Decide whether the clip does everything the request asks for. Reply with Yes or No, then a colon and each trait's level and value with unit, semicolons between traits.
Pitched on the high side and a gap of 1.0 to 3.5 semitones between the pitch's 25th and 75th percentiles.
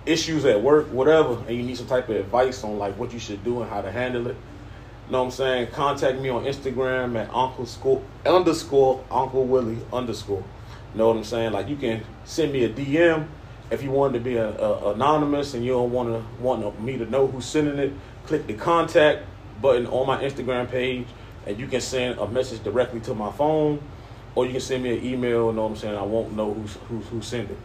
No: low, 125 Hz; average, 2.7 semitones